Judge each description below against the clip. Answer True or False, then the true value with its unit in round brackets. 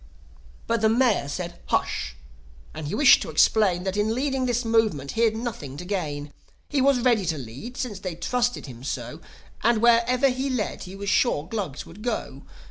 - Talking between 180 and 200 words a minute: True (185 wpm)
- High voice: True (210 Hz)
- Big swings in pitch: True (7.1 semitones)